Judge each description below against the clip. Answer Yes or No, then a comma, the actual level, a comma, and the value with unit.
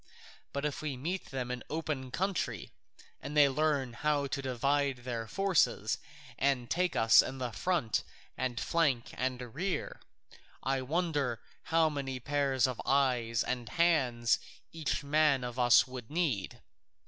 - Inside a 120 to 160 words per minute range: Yes, average, 140 wpm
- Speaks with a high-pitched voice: No, low, 135 Hz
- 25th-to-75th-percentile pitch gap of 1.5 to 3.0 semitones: No, average, 3.6 semitones